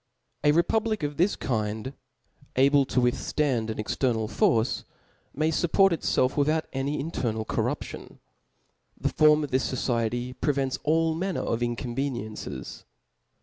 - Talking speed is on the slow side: Yes, slow, 130 wpm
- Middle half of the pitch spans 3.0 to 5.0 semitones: Yes, average, 4.5 semitones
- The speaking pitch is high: No, low, 135 Hz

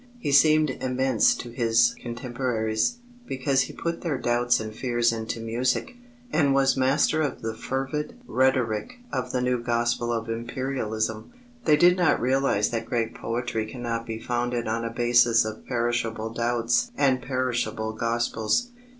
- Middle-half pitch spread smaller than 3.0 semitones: Yes, narrow, 2.5 semitones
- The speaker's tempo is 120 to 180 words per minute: Yes, average, 150 wpm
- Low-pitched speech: Yes, low, 120 Hz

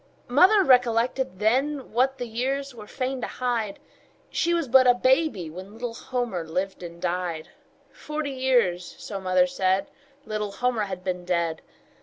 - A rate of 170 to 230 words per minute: No, average, 155 wpm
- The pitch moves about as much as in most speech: No, wide, 6.0 semitones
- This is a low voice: No, high, 230 Hz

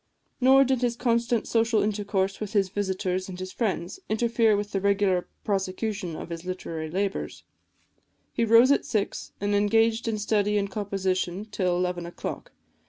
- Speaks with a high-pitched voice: Yes, high, 205 Hz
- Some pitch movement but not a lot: Yes, average, 3.2 semitones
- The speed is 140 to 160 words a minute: Yes, average, 155 wpm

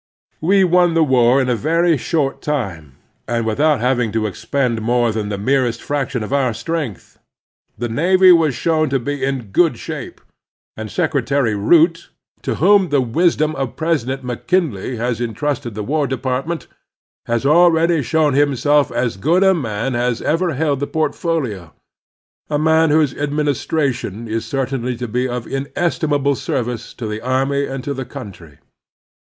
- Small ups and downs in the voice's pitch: No, average, 4.8 semitones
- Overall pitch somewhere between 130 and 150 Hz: Yes, low, 135 Hz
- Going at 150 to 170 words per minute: Yes, average, 165 wpm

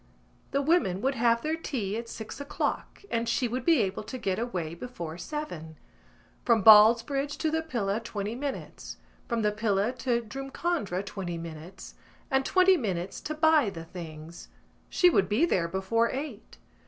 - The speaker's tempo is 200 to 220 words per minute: No, average, 165 wpm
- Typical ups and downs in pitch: No, wide, 6.2 semitones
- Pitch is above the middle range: Yes, high, 230 Hz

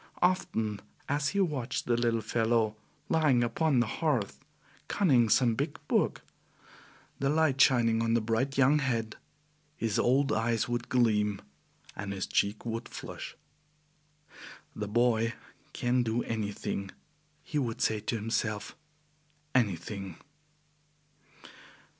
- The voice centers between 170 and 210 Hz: No, low, 115 Hz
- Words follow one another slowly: Yes, slow, 120 wpm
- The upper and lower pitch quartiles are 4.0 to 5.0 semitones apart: No, average, 3.4 semitones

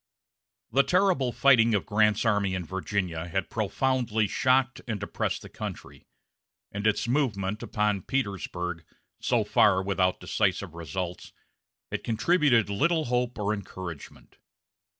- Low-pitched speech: Yes, low, 105 Hz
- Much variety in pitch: No, average, 4.7 semitones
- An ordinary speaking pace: No, slow, 125 wpm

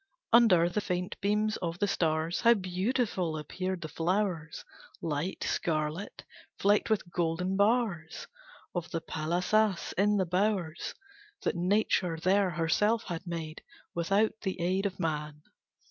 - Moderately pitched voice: Yes, medium, 180 Hz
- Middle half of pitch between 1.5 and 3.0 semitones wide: No, average, 3.7 semitones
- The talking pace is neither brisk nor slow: No, slow, 130 wpm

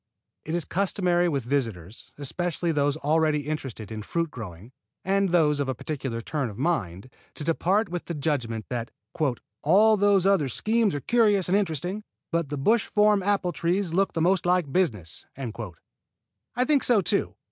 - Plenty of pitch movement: Yes, wide, 6.0 semitones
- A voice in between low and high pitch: Yes, medium, 165 Hz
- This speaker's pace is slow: No, average, 170 wpm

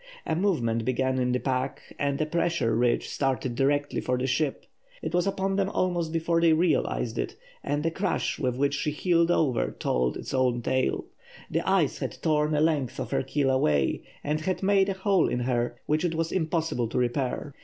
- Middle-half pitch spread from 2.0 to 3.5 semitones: No, average, 4.6 semitones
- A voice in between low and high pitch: Yes, medium, 145 Hz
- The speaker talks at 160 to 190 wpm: No, average, 200 wpm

